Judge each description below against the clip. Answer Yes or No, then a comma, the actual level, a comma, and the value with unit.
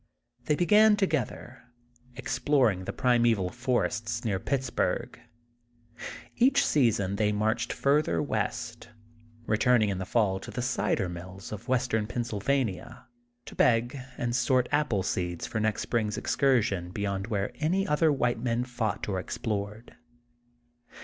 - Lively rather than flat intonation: No, average, 4.1 semitones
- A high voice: No, low, 115 Hz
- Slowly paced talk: Yes, slow, 130 wpm